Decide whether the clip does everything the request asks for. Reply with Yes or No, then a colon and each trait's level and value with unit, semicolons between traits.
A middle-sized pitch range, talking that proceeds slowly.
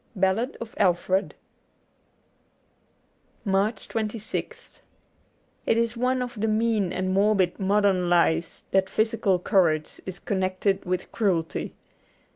Yes: average, 3.0 semitones; slow, 115 wpm